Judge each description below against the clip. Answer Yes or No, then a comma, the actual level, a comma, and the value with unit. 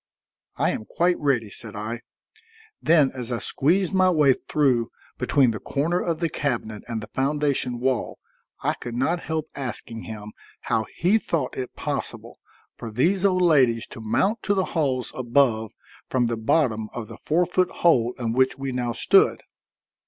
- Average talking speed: Yes, average, 170 wpm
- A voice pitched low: Yes, low, 130 Hz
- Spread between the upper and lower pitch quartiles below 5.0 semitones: No, wide, 5.5 semitones